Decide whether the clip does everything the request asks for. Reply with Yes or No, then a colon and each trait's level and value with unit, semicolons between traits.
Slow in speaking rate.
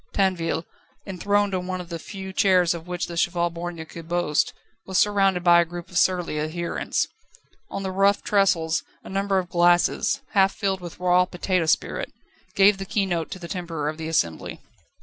No: average, 185 wpm